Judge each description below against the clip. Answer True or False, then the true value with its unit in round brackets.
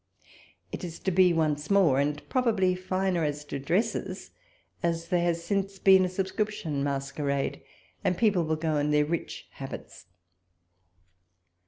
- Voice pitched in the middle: True (170 Hz)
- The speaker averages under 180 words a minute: True (145 wpm)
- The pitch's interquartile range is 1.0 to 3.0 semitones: False (4.3 semitones)